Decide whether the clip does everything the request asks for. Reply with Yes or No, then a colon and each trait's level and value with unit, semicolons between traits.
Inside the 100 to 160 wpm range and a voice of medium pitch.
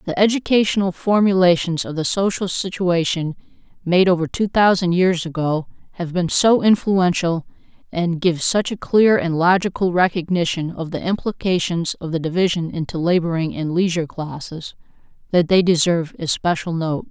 Yes: average, 145 wpm; medium, 175 Hz